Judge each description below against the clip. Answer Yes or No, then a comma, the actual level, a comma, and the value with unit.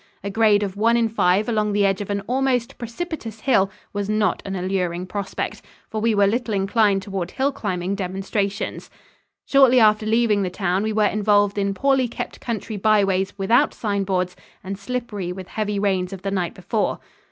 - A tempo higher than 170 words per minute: Yes, average, 185 wpm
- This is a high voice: Yes, high, 205 Hz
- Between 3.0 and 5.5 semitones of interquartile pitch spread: No, narrow, 2.5 semitones